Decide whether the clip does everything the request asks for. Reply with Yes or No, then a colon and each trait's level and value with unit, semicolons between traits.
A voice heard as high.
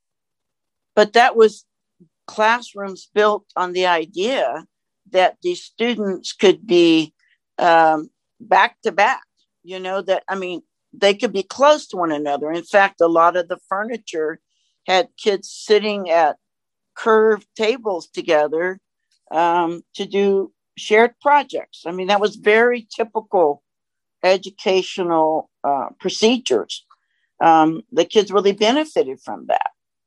Yes: high, 195 Hz